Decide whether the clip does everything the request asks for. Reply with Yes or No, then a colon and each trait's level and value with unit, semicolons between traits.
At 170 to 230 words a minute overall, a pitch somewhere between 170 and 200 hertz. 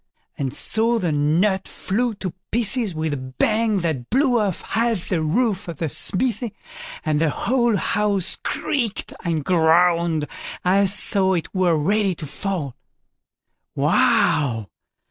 No: slow, 135 wpm; medium, 185 Hz